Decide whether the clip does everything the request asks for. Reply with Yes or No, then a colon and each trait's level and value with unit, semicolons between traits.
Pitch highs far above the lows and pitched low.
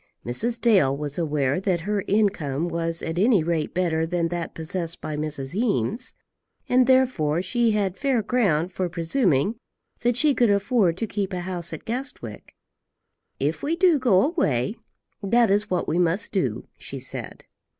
No: wide, 5.9 semitones; medium, 185 Hz